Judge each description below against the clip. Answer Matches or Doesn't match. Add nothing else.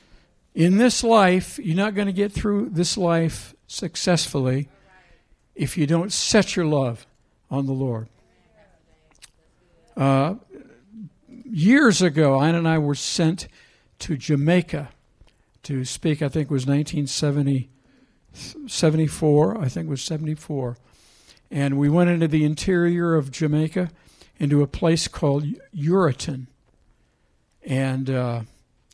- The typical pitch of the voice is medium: Matches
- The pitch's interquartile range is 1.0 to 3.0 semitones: Doesn't match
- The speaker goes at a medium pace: Doesn't match